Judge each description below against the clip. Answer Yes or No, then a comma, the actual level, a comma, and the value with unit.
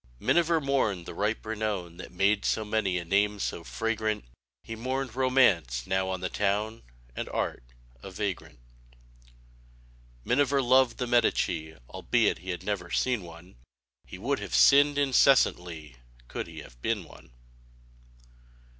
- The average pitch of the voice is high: No, low, 105 Hz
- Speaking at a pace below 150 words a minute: Yes, average, 140 wpm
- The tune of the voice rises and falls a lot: Yes, wide, 5.8 semitones